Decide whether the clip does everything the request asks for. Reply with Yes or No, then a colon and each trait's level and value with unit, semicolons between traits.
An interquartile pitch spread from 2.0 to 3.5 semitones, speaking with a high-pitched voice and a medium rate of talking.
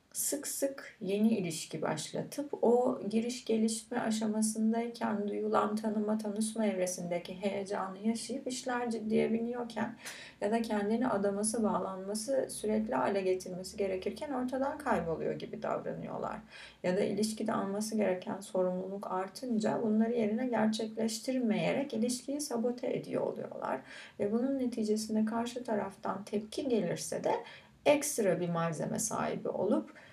Yes: narrow, 2.6 semitones; high, 220 Hz; average, 115 wpm